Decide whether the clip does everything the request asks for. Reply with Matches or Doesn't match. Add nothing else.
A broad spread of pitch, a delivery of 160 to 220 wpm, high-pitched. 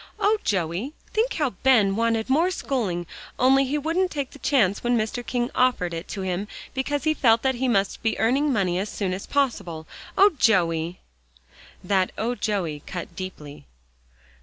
Matches